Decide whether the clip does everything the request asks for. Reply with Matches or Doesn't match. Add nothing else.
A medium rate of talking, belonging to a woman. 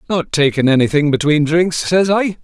Doesn't match